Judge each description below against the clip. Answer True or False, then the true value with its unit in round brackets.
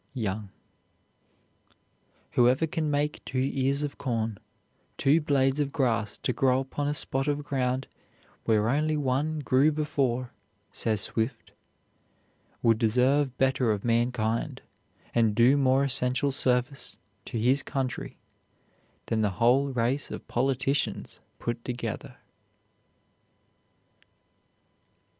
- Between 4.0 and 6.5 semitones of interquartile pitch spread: False (2.9 semitones)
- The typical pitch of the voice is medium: False (130 Hz)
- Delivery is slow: True (110 wpm)